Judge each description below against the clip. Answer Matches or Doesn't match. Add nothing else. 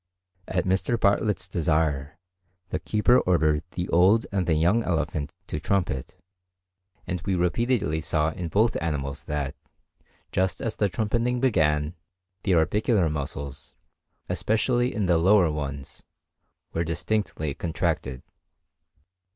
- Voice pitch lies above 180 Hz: Doesn't match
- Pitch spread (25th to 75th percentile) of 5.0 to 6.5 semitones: Matches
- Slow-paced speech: Matches